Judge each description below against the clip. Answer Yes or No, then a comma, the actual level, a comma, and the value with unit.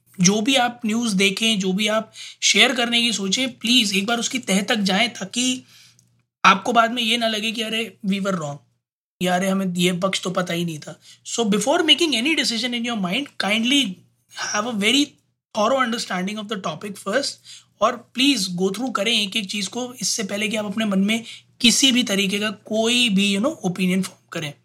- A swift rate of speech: Yes, fast, 205 wpm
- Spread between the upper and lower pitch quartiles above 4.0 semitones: No, average, 3.7 semitones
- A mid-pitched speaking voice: No, high, 215 Hz